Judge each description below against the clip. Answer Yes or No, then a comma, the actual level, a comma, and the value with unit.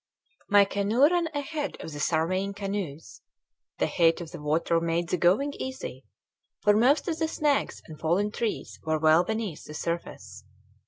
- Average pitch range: No, wide, 7.9 semitones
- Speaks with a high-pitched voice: Yes, high, 195 Hz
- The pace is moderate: Yes, average, 165 wpm